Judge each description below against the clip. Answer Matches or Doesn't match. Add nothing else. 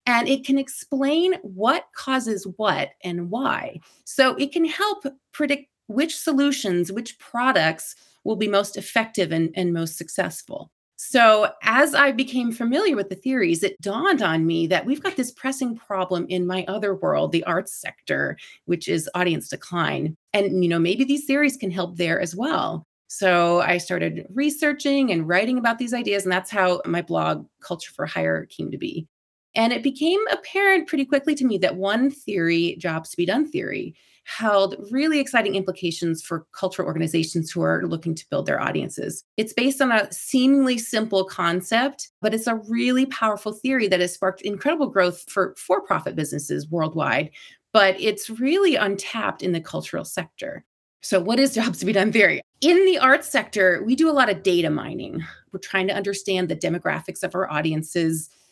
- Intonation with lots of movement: Matches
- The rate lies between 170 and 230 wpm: Matches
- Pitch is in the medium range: Doesn't match